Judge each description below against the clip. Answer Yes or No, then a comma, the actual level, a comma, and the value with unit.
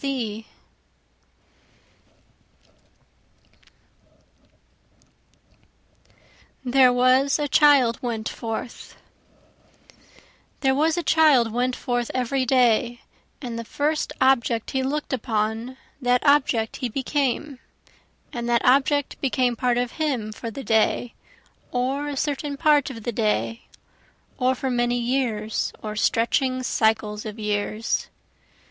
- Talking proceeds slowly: Yes, slow, 105 wpm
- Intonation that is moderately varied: Yes, average, 3.0 semitones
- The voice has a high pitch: Yes, very high, 250 Hz